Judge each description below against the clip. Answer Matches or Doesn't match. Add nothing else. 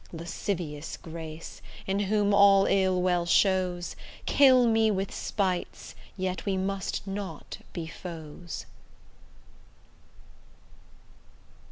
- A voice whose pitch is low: Doesn't match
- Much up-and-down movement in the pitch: Doesn't match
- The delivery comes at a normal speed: Doesn't match